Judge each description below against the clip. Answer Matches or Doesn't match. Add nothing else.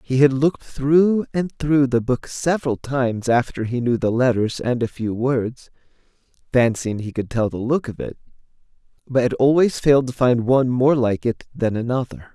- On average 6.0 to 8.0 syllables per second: Doesn't match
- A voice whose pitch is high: Doesn't match